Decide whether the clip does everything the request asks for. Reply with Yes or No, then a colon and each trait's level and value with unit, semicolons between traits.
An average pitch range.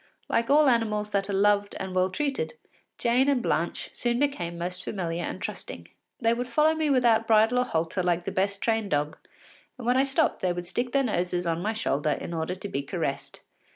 No: wide, 5.7 semitones